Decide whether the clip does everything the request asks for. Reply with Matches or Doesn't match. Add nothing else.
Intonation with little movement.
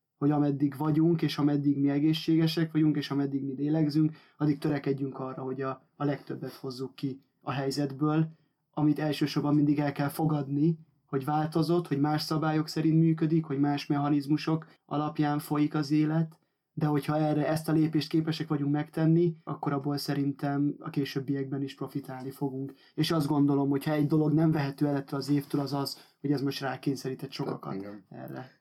Matches